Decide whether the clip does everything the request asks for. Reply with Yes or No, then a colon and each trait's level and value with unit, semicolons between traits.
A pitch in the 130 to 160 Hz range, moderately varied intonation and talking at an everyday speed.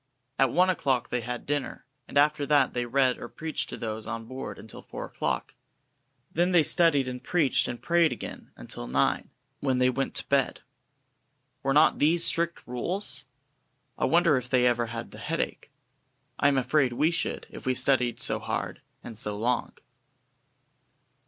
Yes: low, 135 Hz; average, 3.9 semitones; average, 170 wpm